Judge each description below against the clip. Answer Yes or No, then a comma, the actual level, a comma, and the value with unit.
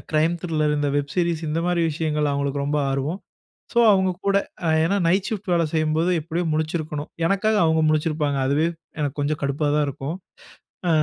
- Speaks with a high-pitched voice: No, medium, 155 Hz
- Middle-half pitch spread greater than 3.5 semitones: No, narrow, 2.5 semitones